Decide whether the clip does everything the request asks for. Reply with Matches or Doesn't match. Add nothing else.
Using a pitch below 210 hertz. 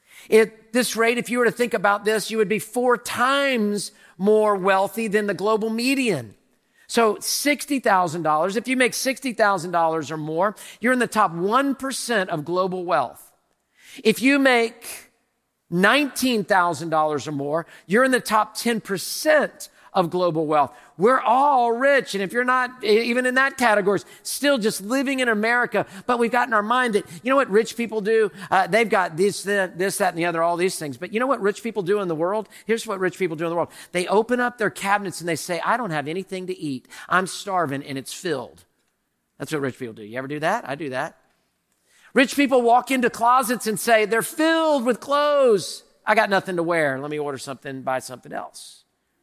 Doesn't match